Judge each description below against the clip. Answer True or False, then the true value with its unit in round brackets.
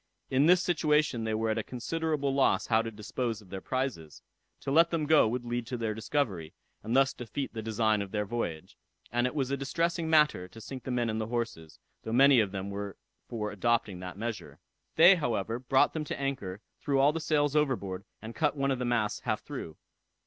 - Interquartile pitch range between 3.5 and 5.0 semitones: True (4.5 semitones)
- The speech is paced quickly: True (215 wpm)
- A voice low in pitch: True (120 Hz)